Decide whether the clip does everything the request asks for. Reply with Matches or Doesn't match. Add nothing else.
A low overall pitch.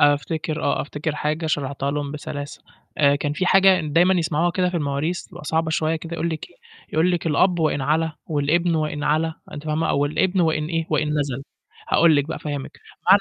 Doesn't match